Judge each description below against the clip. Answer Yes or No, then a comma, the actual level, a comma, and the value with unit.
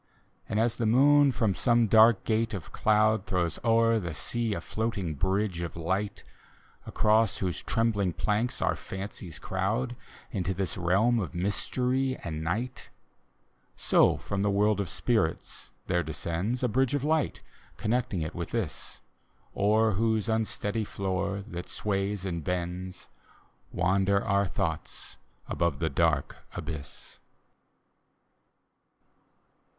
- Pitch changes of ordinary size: Yes, average, 4.0 semitones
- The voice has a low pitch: Yes, low, 100 Hz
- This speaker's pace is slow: Yes, slow, 130 wpm